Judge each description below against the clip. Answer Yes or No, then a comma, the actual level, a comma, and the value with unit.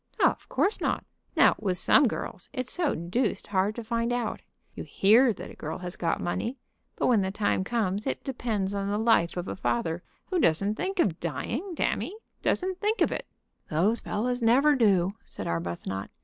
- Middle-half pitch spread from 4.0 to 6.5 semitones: Yes, wide, 5.6 semitones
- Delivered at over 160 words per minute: Yes, average, 190 wpm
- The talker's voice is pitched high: Yes, high, 210 Hz